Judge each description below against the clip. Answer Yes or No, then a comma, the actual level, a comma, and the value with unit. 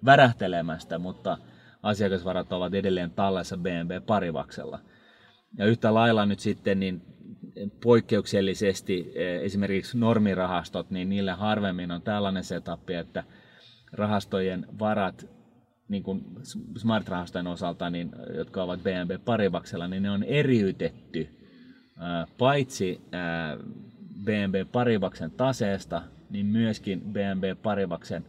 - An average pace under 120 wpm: Yes, average, 100 wpm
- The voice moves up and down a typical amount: Yes, average, 3.1 semitones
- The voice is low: Yes, low, 100 Hz